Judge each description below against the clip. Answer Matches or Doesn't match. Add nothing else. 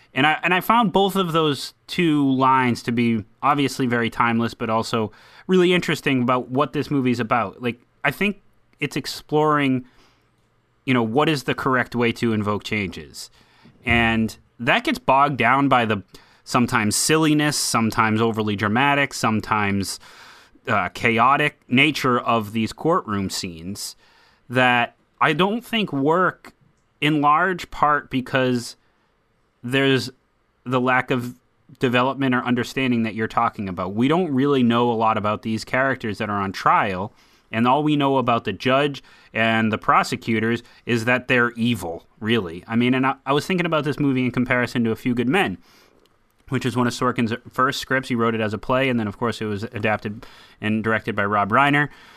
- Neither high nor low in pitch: Doesn't match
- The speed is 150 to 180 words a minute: Matches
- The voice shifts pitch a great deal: Doesn't match